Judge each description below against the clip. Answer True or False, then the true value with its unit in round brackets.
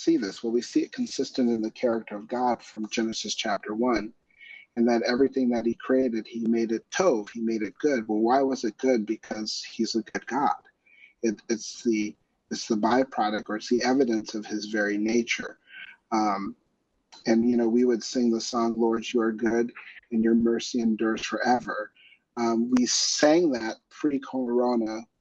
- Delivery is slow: False (185 wpm)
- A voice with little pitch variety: True (1.8 semitones)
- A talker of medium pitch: False (115 Hz)